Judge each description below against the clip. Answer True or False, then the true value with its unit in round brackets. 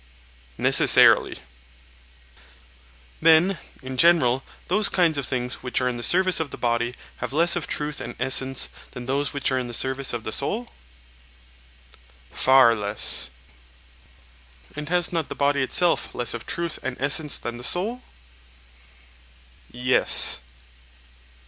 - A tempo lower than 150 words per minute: True (135 wpm)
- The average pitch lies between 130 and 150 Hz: True (135 Hz)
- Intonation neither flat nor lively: True (5.0 semitones)